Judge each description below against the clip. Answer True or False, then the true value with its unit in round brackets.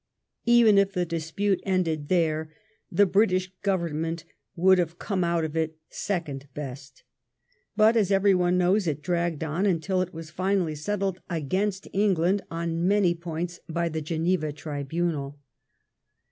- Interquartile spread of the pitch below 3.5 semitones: True (3.1 semitones)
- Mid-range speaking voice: True (175 Hz)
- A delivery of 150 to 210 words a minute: False (140 wpm)